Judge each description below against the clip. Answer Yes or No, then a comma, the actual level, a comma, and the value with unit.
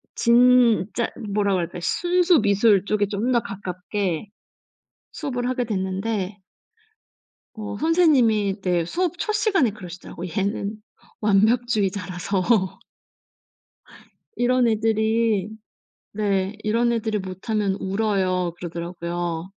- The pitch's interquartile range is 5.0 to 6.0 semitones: No, average, 3.8 semitones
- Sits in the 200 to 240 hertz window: Yes, high, 210 Hz